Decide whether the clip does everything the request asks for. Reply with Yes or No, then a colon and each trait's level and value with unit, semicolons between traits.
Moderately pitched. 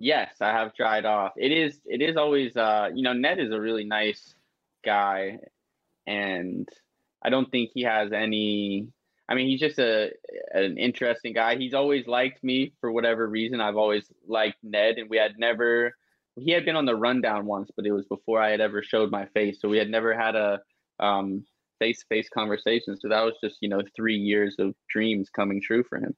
No: low, 110 Hz